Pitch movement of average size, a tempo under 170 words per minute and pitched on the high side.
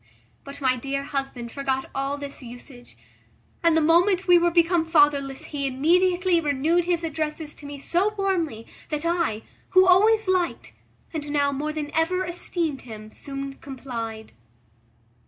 Yes: average, 4.1 semitones; average, 150 wpm; very high, 300 Hz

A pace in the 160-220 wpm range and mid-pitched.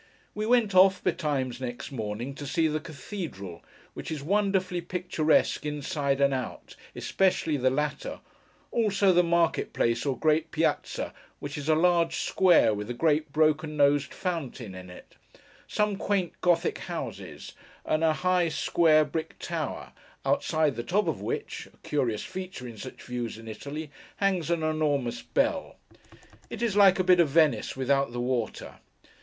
No: average, 150 wpm; medium, 155 Hz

